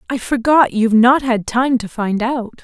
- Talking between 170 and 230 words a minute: Yes, fast, 205 wpm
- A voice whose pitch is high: Yes, high, 240 Hz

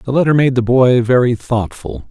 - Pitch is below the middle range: Yes, low, 125 Hz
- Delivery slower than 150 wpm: No, average, 200 wpm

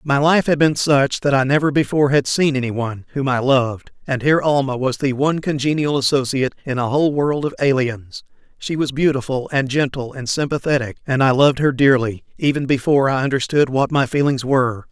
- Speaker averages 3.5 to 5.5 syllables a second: No, 5.8 syllables/s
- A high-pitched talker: No, low, 135 Hz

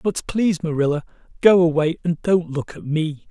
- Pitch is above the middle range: No, medium, 165 Hz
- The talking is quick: No, average, 180 wpm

